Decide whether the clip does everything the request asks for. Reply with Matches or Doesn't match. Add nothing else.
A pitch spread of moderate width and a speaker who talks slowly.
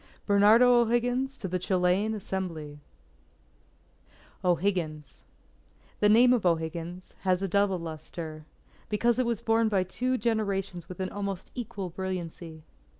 Matches